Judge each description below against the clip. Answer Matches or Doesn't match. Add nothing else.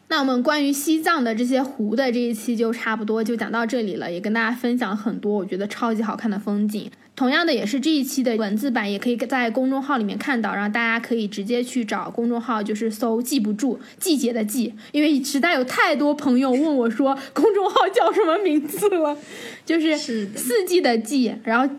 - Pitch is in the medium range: Doesn't match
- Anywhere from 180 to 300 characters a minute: Doesn't match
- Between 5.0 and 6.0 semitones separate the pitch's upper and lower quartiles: Doesn't match